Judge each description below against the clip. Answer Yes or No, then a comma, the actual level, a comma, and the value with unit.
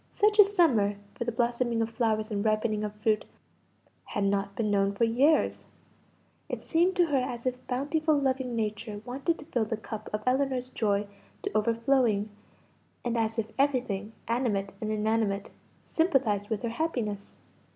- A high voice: Yes, high, 230 Hz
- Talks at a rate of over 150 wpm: Yes, average, 160 wpm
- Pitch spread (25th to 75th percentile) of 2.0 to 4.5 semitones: Yes, average, 3.7 semitones